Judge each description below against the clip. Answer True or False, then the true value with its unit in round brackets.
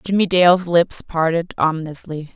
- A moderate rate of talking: False (130 wpm)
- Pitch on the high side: False (170 Hz)